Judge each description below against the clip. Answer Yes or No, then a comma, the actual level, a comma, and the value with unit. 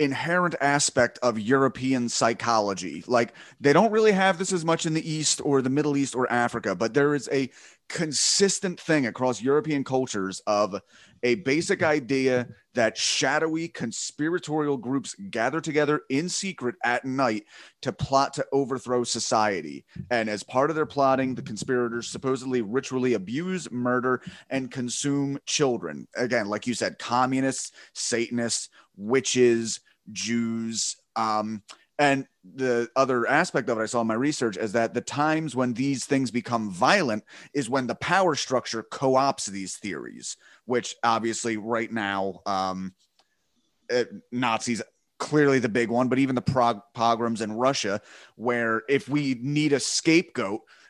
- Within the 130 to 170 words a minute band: Yes, average, 150 wpm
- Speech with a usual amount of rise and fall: Yes, average, 3.5 semitones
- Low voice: Yes, low, 130 Hz